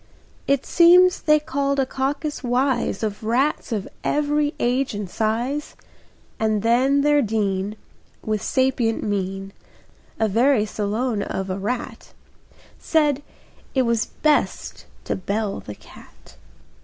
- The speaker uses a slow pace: Yes, slow, 125 wpm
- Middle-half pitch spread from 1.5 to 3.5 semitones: No, average, 4.9 semitones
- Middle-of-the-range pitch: No, high, 240 Hz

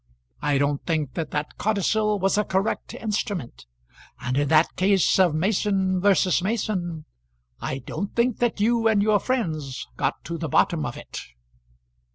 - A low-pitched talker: No, medium, 185 Hz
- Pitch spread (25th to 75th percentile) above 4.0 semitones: Yes, average, 5.3 semitones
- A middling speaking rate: Yes, average, 160 wpm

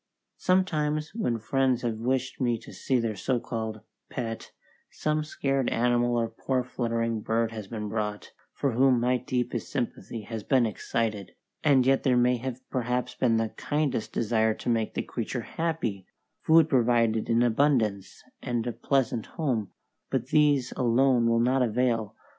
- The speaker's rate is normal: Yes, average, 160 wpm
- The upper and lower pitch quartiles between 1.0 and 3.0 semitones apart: Yes, average, 2.7 semitones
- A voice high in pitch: No, low, 120 Hz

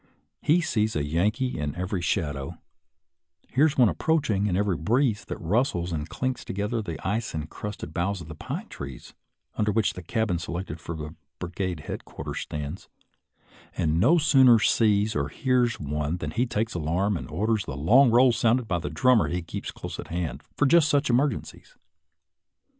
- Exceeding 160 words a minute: Yes, average, 170 wpm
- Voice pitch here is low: Yes, low, 100 Hz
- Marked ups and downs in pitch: Yes, wide, 6.3 semitones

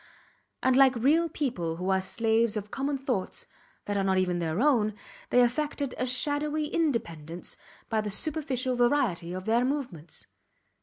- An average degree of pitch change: No, wide, 6.6 semitones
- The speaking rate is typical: Yes, average, 155 wpm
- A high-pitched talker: Yes, high, 240 Hz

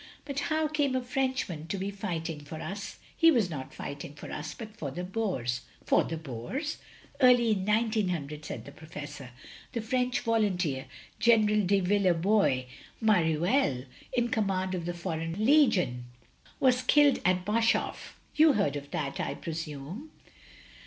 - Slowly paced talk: No, average, 155 wpm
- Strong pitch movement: Yes, wide, 6.9 semitones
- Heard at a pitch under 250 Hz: Yes, high, 190 Hz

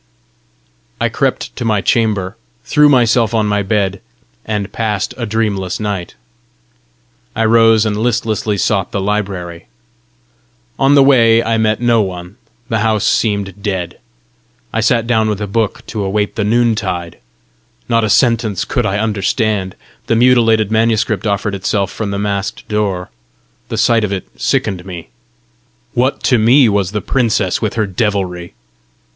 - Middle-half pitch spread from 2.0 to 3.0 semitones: Yes, narrow, 2.5 semitones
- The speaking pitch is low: Yes, low, 105 Hz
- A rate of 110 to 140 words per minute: No, average, 150 wpm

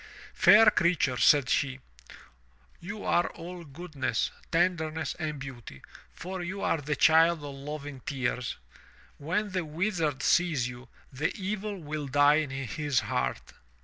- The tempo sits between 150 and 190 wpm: No, slow, 135 wpm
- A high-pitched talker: No, medium, 155 Hz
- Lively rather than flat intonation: No, average, 4.2 semitones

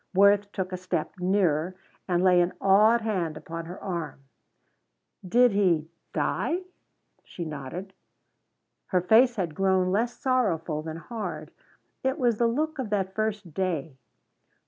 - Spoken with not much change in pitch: No, average, 4.2 semitones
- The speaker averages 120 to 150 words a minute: Yes, average, 140 wpm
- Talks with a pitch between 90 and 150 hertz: No, high, 190 Hz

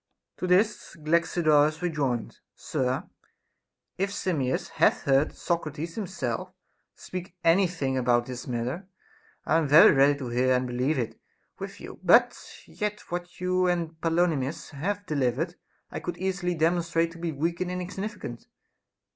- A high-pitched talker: No, medium, 165 Hz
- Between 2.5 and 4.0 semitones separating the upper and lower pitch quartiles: No, average, 4.9 semitones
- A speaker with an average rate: Yes, average, 145 wpm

